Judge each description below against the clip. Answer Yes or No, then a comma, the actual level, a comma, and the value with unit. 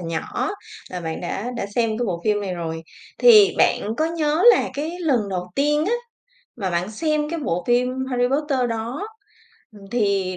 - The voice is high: Yes, high, 240 Hz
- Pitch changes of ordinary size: No, wide, 7.8 semitones